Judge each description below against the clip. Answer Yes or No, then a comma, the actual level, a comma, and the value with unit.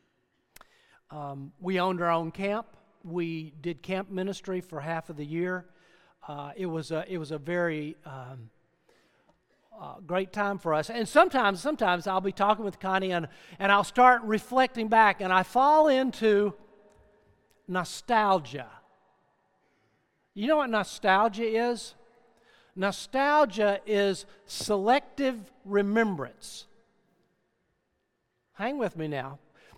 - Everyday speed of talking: No, slow, 125 wpm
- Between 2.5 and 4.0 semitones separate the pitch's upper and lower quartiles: No, average, 4.6 semitones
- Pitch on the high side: Yes, high, 195 Hz